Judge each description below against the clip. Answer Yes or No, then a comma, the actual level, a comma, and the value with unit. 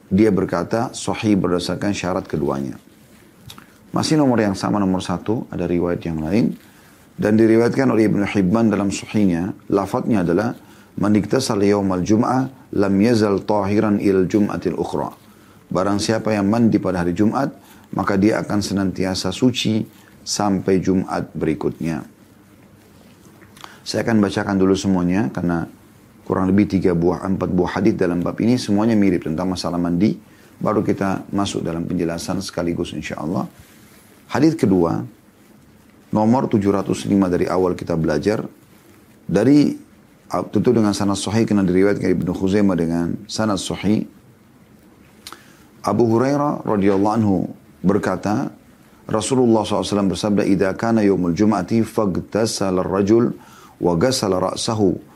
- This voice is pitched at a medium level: No, low, 100 Hz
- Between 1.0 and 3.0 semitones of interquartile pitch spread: Yes, average, 2.7 semitones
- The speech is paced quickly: No, average, 120 wpm